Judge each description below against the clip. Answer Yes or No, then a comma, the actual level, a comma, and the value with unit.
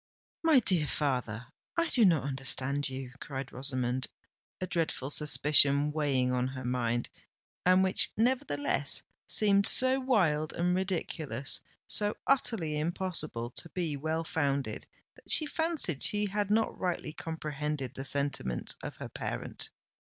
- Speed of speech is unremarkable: No, slow, 130 wpm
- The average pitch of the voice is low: No, medium, 150 Hz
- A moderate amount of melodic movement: No, wide, 5.8 semitones